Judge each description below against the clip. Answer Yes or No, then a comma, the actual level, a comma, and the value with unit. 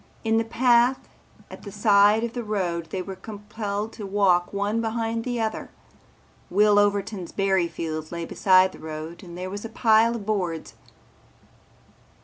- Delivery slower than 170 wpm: Yes, average, 160 wpm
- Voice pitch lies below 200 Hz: No, high, 205 Hz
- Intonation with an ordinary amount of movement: Yes, average, 3.2 semitones